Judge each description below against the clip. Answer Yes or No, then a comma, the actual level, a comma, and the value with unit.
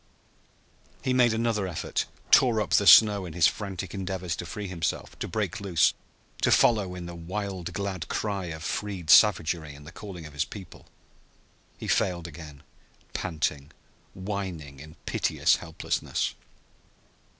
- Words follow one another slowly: No, average, 145 wpm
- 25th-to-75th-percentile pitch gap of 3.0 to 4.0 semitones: Yes, average, 3.6 semitones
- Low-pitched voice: Yes, very low, 90 Hz